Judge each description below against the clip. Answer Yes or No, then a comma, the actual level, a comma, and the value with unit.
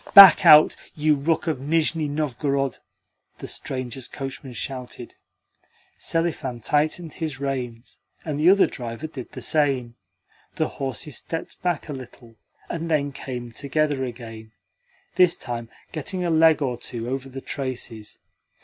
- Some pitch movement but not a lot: Yes, average, 3.9 semitones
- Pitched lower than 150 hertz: Yes, medium, 140 Hz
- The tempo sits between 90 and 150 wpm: Yes, average, 140 wpm